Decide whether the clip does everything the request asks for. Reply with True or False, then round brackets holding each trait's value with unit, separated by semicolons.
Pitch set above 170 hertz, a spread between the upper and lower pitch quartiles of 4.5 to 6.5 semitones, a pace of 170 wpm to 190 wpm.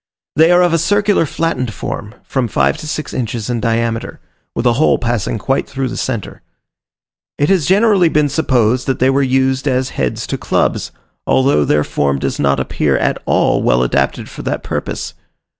False (130 Hz; 5.1 semitones; 185 wpm)